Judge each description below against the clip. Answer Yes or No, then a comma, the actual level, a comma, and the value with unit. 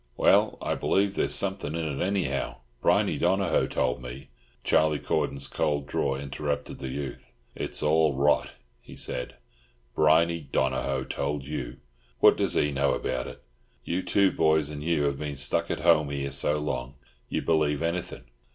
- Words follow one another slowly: No, average, 160 wpm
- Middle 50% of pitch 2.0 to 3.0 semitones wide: Yes, narrow, 2.6 semitones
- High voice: No, very low, 75 Hz